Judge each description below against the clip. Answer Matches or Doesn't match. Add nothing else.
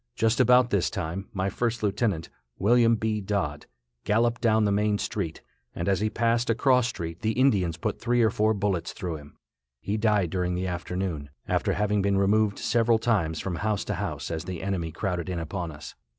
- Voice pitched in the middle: Doesn't match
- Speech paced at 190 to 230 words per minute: Matches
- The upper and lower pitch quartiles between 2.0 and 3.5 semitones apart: Doesn't match